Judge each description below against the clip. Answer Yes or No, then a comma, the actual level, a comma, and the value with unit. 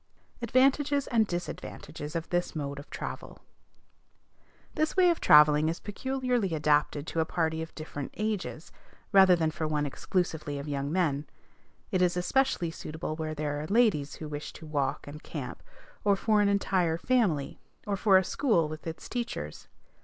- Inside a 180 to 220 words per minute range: No, average, 165 wpm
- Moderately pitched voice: Yes, medium, 165 Hz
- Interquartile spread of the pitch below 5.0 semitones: No, wide, 5.5 semitones